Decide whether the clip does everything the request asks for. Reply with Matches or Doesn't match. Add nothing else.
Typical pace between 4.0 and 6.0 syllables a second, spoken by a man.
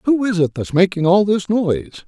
Matches